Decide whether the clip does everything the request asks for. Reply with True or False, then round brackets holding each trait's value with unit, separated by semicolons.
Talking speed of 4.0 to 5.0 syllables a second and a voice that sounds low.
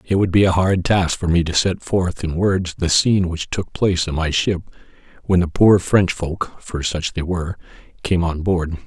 True (4.6 syllables/s; 90 Hz)